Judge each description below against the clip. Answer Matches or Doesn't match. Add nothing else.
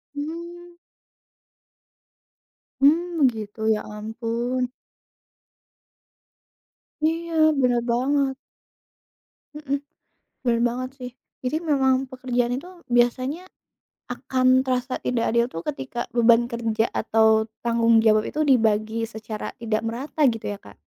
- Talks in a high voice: Matches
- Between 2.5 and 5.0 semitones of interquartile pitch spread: Matches